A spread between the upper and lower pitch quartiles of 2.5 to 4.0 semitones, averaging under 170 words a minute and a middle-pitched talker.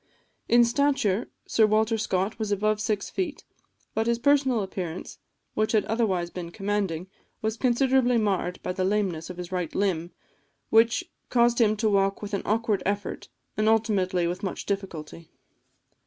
No: average, 3.5 semitones; average, 155 wpm; high, 210 Hz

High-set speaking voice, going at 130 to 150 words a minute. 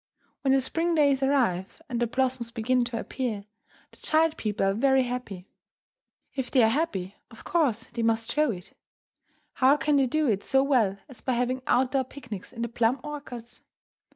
No: very high, 250 Hz; average, 185 wpm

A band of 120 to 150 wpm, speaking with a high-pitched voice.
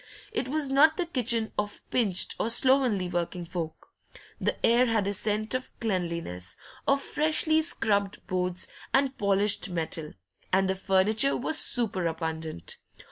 Yes: average, 140 wpm; high, 205 Hz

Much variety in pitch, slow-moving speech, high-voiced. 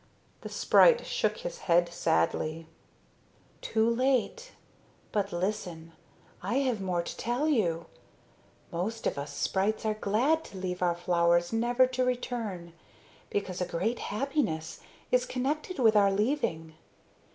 Yes: wide, 6.5 semitones; slow, 130 wpm; high, 210 Hz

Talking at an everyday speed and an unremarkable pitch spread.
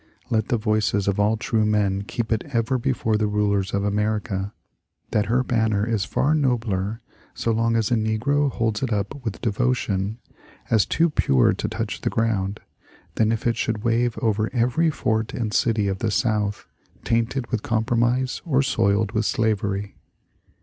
No: average, 175 wpm; narrow, 2.2 semitones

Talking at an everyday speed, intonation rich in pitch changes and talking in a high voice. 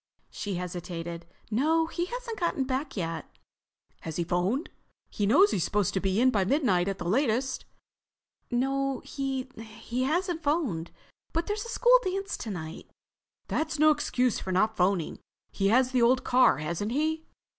Yes: average, 155 wpm; wide, 8.4 semitones; very high, 250 Hz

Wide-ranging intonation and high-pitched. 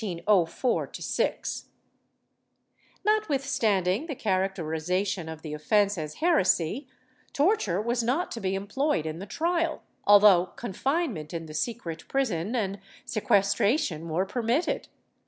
Yes: wide, 6.9 semitones; high, 200 Hz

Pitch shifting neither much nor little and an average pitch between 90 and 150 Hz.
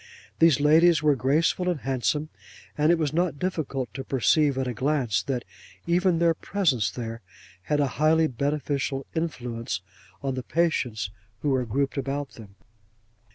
Yes: average, 4.0 semitones; medium, 140 Hz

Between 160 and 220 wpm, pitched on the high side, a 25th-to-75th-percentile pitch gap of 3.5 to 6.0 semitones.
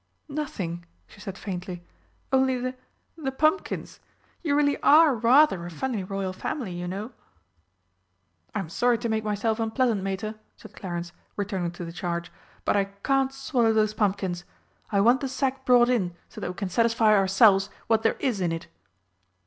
Yes: average, 165 wpm; high, 215 Hz; average, 5.2 semitones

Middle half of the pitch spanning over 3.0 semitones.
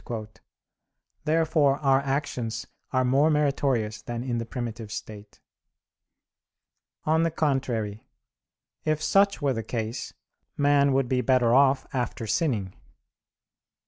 Yes: average, 3.8 semitones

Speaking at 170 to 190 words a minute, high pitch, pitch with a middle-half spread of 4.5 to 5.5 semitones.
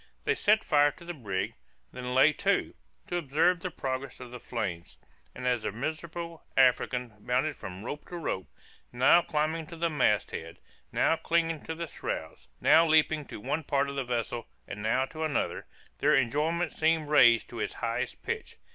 No: average, 180 wpm; medium, 145 Hz; average, 4.8 semitones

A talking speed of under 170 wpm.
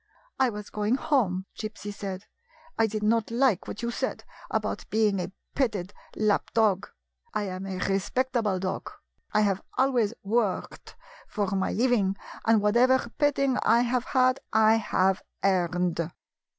Yes: average, 150 wpm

